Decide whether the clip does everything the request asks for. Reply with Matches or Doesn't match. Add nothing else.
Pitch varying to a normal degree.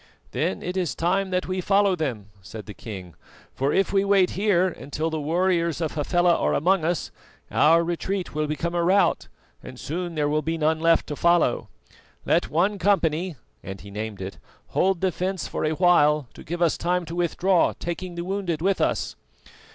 Matches